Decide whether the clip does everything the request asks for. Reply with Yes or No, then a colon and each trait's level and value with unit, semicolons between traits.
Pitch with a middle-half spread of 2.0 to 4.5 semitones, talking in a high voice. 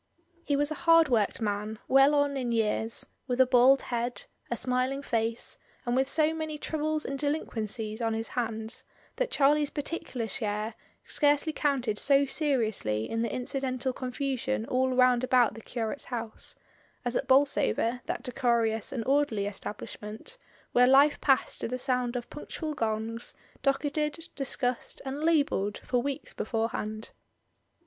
Yes: average, 3.8 semitones; very high, 255 Hz